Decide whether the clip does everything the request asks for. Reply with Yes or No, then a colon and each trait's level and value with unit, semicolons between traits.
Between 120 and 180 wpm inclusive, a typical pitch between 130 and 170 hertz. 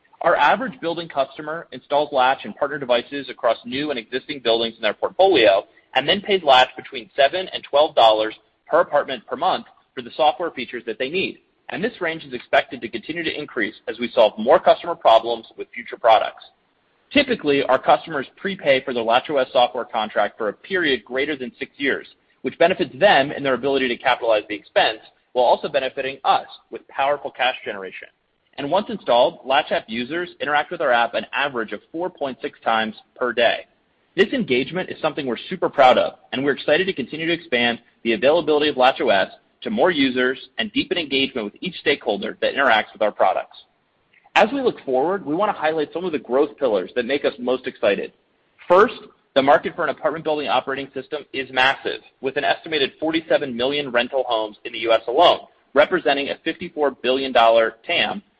No: average, 190 wpm; medium, 140 Hz